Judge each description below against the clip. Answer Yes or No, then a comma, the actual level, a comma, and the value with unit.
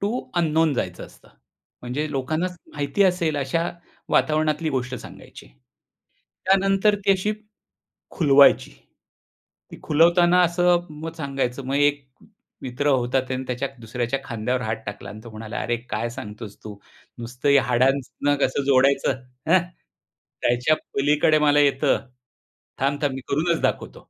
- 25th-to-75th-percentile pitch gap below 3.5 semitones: No, average, 4.1 semitones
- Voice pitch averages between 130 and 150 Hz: Yes, medium, 140 Hz